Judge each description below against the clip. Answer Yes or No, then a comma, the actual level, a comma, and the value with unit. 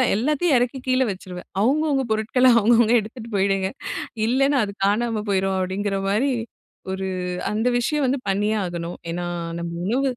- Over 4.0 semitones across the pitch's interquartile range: Yes, average, 4.9 semitones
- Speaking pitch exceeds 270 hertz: No, high, 220 Hz